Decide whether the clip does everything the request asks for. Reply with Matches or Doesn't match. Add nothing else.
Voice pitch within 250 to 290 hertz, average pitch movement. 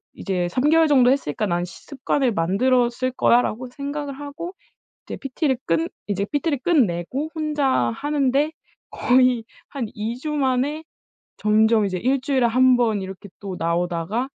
Doesn't match